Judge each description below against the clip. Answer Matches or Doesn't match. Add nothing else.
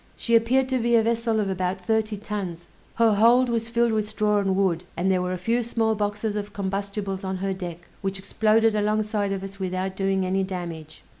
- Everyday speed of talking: Doesn't match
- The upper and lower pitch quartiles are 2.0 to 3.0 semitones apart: Matches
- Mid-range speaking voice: Doesn't match